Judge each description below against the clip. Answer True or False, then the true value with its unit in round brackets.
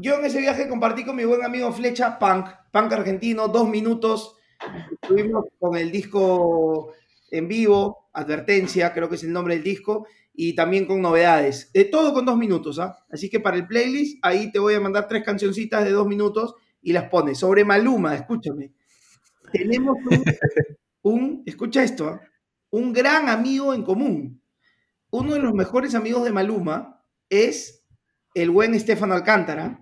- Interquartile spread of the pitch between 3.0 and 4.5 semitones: False (5.1 semitones)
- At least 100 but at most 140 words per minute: False (165 wpm)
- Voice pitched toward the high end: True (210 Hz)